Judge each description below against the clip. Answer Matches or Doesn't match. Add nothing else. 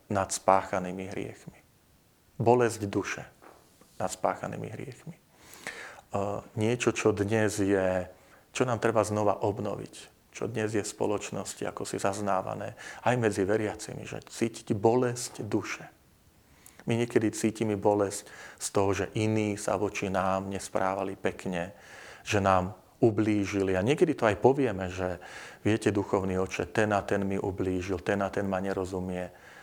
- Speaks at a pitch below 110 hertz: Matches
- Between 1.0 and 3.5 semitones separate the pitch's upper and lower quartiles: Matches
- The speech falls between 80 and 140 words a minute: Matches